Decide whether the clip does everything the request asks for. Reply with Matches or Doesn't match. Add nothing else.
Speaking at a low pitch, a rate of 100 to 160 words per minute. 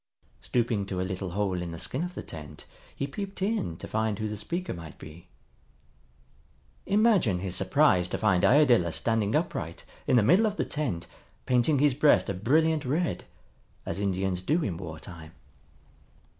Doesn't match